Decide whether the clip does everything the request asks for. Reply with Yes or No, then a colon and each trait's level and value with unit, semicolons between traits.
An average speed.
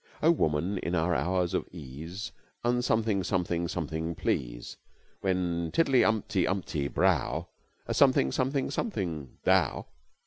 No: slow, 130 wpm